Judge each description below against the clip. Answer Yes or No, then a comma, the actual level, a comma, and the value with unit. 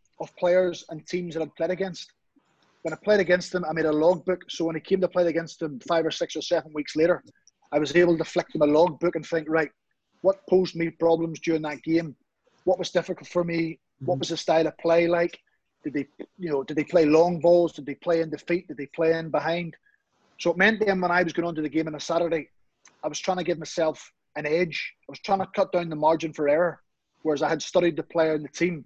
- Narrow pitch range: Yes, narrow, 2.1 semitones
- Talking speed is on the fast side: Yes, fast, 260 wpm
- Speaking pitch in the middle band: Yes, medium, 165 Hz